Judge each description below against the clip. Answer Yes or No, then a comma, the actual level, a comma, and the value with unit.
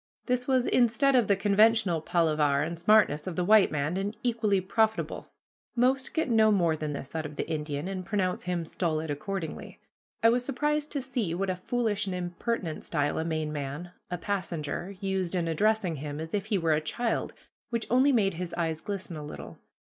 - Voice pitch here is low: No, medium, 185 Hz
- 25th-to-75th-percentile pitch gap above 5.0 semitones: Yes, wide, 5.6 semitones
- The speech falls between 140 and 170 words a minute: No, average, 195 wpm